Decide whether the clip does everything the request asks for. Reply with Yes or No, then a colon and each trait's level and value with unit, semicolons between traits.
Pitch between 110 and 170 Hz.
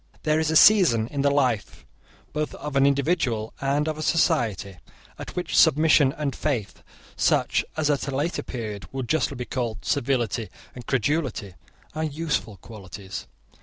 Yes: medium, 140 Hz